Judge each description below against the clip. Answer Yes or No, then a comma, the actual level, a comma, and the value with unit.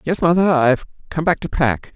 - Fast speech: Yes, fast, 215 wpm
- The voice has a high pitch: No, medium, 155 Hz